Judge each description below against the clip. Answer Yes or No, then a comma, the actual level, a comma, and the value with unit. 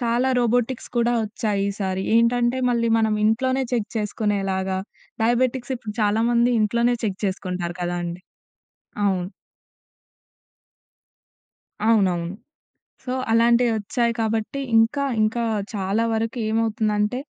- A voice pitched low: No, high, 225 Hz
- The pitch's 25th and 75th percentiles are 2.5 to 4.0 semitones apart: Yes, average, 2.9 semitones